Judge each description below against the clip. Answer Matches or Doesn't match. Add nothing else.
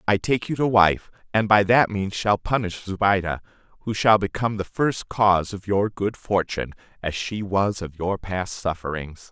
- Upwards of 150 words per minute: Matches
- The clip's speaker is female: Doesn't match